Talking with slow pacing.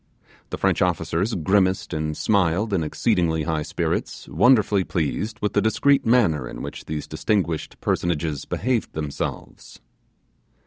Yes: slow, 130 wpm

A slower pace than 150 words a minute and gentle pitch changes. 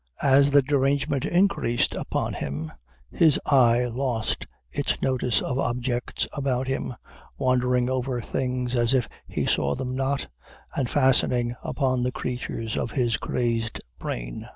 Yes: slow, 135 wpm; narrow, 1.9 semitones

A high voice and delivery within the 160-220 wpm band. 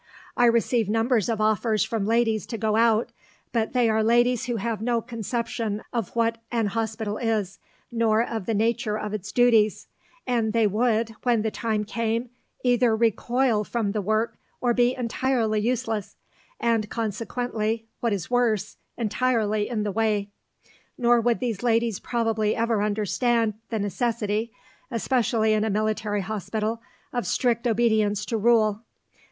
No: high, 225 Hz; average, 150 wpm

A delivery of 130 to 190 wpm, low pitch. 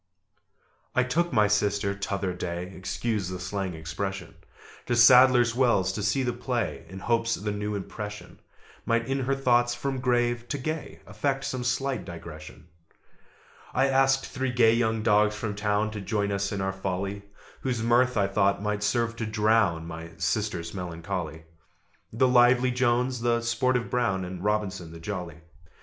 Yes: average, 160 wpm; low, 105 Hz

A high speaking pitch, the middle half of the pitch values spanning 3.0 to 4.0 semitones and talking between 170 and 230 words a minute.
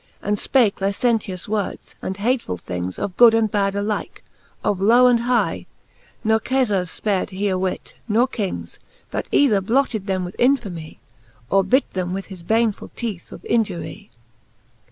No: high, 205 Hz; average, 3.7 semitones; average, 155 wpm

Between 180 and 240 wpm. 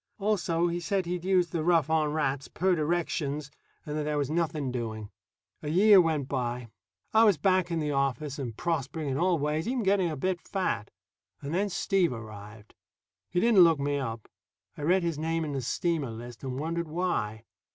Yes: average, 195 wpm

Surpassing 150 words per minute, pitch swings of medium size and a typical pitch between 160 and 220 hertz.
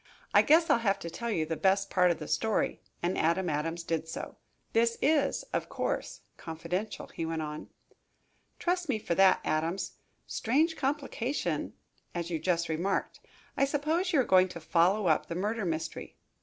No: average, 175 wpm; wide, 6.2 semitones; medium, 185 Hz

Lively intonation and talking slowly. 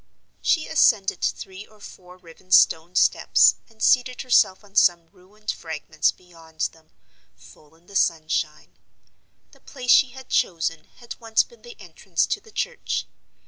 No: wide, 6.6 semitones; average, 150 wpm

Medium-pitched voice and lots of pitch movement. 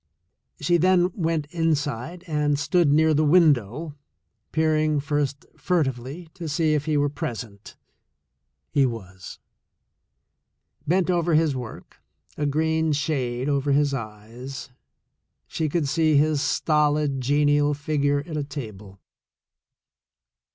No: medium, 145 Hz; average, 2.7 semitones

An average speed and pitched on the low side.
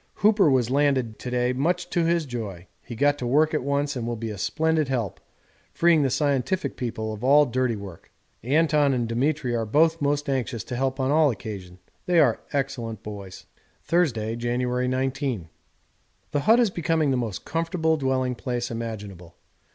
Yes: average, 175 wpm; low, 130 Hz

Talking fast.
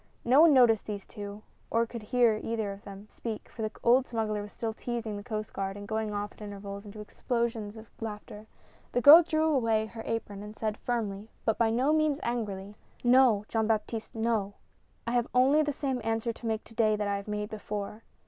Yes: fast, 220 wpm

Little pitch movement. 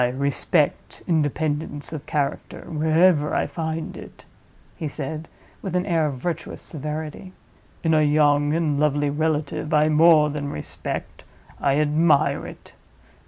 Yes: narrow, 1.6 semitones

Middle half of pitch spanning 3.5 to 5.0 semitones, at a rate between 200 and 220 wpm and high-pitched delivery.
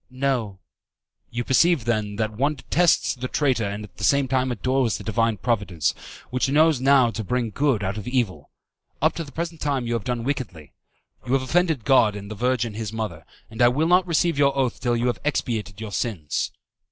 No: average, 4.3 semitones; fast, 205 wpm; low, 125 Hz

